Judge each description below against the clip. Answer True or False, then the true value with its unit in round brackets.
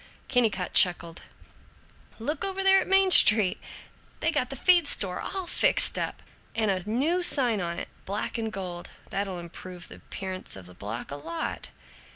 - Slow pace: False (170 wpm)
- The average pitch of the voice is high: True (205 Hz)